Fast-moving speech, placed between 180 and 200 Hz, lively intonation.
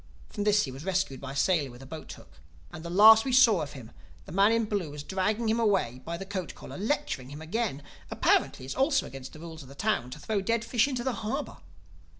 Yes: fast, 250 wpm; high, 190 Hz; wide, 7.4 semitones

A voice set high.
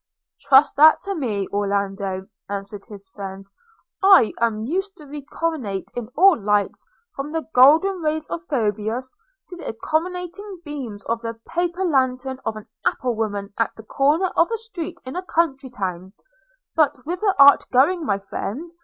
Yes: very high, 270 Hz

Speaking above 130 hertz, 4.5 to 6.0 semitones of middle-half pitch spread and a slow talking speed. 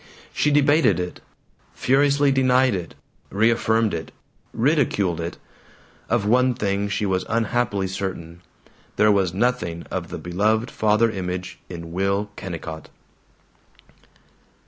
No: low, 105 Hz; average, 4.8 semitones; slow, 115 wpm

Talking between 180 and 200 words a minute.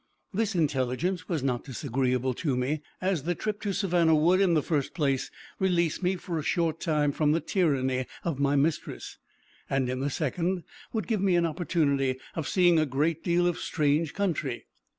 Yes: average, 185 wpm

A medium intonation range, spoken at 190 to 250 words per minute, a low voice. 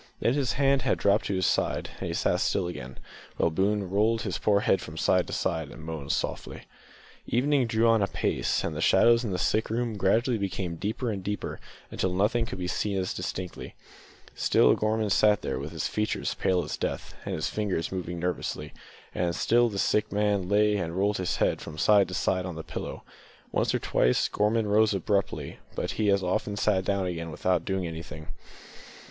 Yes: average, 3.2 semitones; average, 195 wpm; low, 100 Hz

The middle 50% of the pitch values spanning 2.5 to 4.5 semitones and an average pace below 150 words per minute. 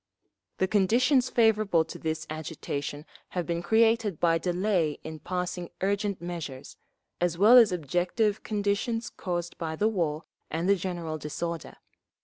Yes: average, 4.0 semitones; slow, 135 wpm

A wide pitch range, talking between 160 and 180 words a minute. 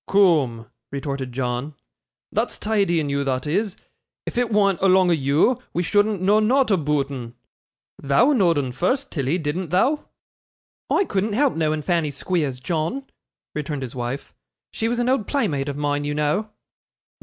Yes: wide, 6.7 semitones; average, 165 wpm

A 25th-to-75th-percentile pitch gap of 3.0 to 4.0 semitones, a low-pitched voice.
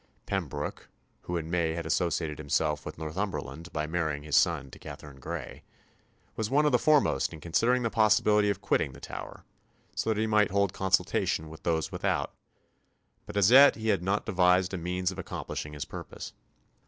No: average, 4.9 semitones; very low, 90 Hz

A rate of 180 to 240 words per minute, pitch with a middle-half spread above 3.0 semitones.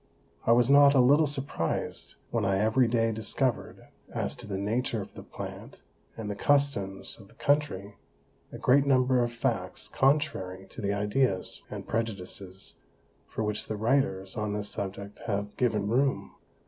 No: average, 160 wpm; average, 4.6 semitones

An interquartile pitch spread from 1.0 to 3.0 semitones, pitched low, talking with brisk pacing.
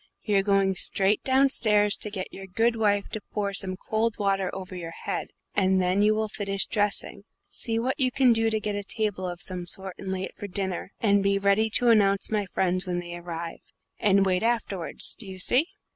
No: narrow, 2.4 semitones; high, 200 Hz; fast, 210 wpm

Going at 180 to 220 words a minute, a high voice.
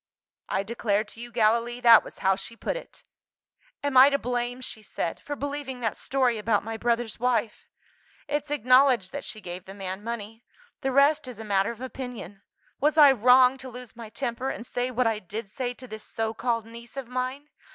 Yes: fast, 205 wpm; high, 240 Hz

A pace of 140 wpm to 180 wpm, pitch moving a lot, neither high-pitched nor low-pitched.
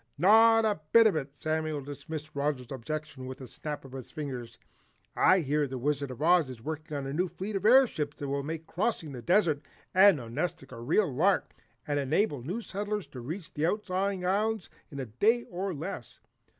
No: average, 195 wpm; wide, 5.7 semitones; medium, 155 Hz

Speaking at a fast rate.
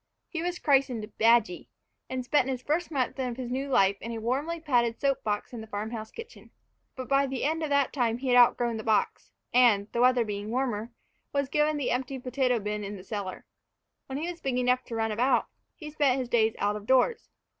Yes: fast, 220 wpm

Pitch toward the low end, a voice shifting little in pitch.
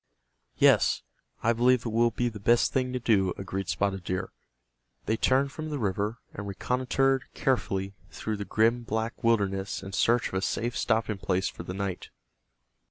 No: low, 110 Hz; average, 3.9 semitones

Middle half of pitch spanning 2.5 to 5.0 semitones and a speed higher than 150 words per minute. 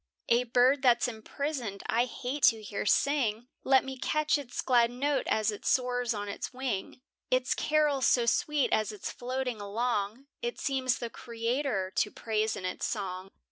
Yes: average, 3.5 semitones; average, 170 wpm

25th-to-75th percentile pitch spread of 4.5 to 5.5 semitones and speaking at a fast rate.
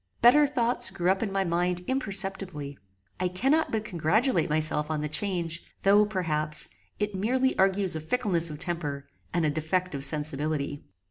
No: average, 5.1 semitones; average, 160 wpm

